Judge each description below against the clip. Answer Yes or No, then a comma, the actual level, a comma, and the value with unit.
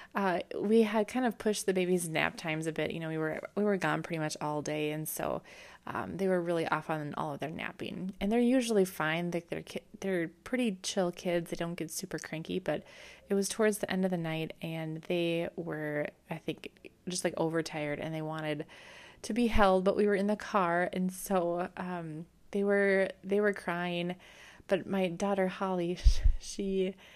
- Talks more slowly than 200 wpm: No, fast, 205 wpm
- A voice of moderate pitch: Yes, medium, 180 Hz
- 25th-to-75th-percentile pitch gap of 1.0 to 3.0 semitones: No, average, 3.6 semitones